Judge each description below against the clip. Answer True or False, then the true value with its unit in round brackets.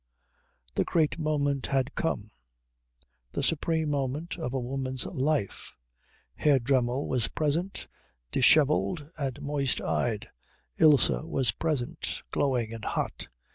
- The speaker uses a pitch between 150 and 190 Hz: False (140 Hz)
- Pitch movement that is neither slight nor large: True (3.3 semitones)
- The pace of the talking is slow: True (115 wpm)